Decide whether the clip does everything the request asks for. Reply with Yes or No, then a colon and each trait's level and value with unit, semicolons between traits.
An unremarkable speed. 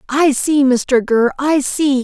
Yes: average, 175 wpm